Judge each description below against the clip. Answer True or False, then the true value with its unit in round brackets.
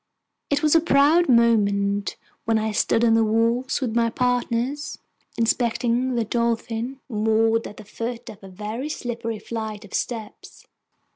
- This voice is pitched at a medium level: False (230 Hz)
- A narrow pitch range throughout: True (2.2 semitones)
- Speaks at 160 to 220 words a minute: False (150 wpm)